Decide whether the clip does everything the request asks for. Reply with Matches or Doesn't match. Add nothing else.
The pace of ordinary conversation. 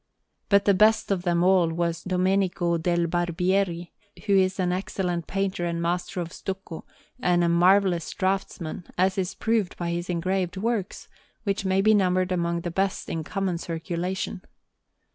Matches